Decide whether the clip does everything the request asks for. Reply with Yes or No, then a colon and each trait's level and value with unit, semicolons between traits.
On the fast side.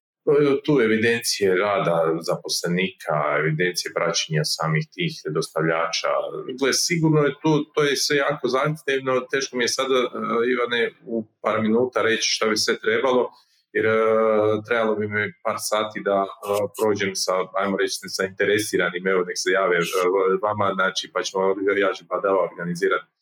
No: average, 145 wpm